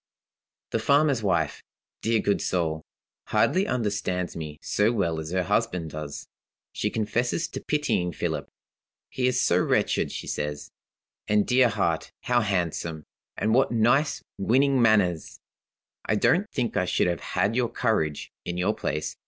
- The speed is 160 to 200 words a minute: No, average, 150 wpm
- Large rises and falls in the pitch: Yes, wide, 6.1 semitones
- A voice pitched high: No, low, 105 Hz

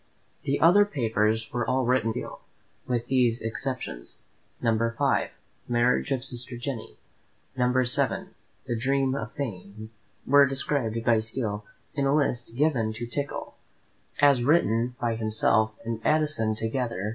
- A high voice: No, low, 120 Hz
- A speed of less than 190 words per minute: Yes, average, 145 wpm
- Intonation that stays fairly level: No, average, 3.3 semitones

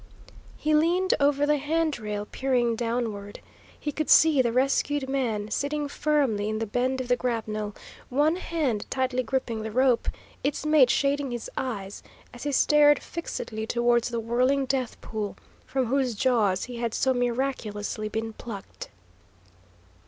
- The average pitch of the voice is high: Yes, very high, 250 Hz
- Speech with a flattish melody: No, average, 4.1 semitones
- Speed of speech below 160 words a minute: Yes, average, 150 wpm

